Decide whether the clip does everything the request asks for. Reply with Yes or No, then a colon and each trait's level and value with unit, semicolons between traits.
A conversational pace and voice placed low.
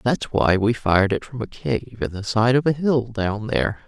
No: fast, 250 wpm; low, 115 Hz